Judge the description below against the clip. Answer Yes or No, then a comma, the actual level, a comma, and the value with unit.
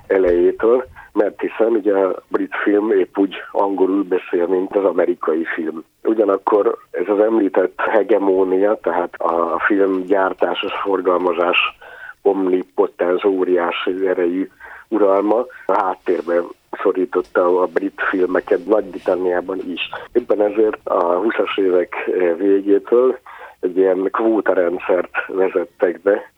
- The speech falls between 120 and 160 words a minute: No, average, 110 wpm